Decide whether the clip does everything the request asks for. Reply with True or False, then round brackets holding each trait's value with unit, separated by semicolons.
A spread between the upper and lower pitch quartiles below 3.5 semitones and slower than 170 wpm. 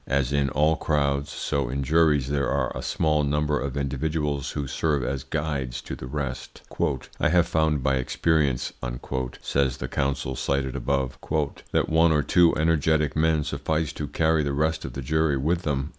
False (2.4 semitones; 175 wpm)